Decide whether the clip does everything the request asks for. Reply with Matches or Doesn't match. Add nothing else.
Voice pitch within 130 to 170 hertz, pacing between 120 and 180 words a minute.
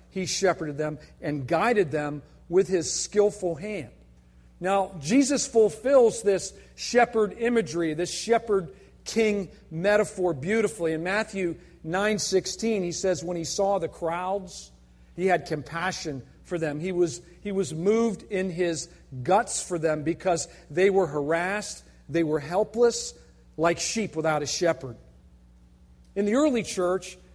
Doesn't match